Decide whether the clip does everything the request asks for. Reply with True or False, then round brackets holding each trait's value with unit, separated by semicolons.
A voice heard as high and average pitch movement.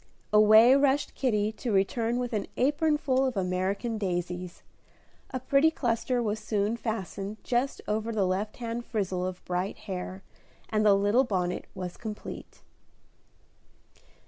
True (215 Hz; 4.0 semitones)